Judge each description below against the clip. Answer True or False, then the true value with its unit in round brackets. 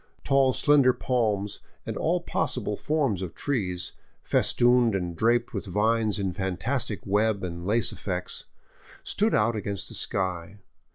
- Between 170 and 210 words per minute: False (135 wpm)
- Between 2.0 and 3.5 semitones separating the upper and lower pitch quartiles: False (4.3 semitones)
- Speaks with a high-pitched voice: False (105 Hz)